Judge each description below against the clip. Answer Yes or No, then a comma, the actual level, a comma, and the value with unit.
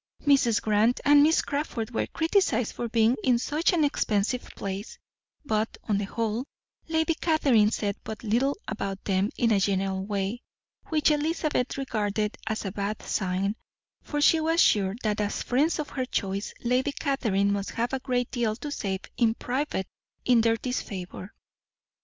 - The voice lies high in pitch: Yes, high, 230 Hz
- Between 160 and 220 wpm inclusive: Yes, average, 165 wpm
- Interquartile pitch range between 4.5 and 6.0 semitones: Yes, average, 5.2 semitones